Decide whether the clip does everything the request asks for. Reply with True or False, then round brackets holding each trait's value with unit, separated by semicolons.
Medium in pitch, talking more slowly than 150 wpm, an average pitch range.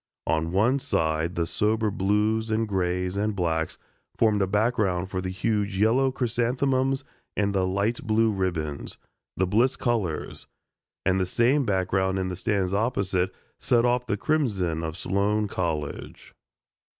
False (100 Hz; 140 wpm; 3.6 semitones)